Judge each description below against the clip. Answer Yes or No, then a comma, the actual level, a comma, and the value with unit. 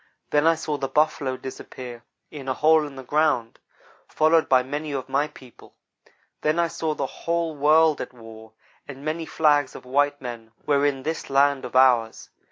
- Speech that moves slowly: No, average, 180 wpm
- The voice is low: No, medium, 145 Hz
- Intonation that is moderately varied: Yes, average, 3.0 semitones